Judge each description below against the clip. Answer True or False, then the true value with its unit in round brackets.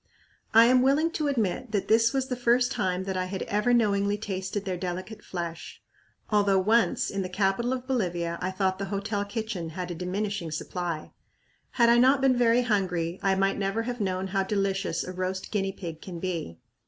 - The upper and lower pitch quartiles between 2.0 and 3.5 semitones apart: False (3.9 semitones)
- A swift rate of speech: False (195 wpm)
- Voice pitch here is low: False (195 Hz)